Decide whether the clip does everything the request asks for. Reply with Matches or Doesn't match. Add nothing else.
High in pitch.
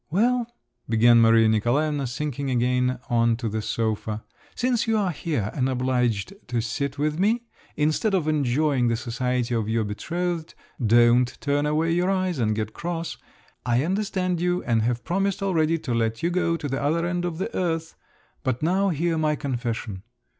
Doesn't match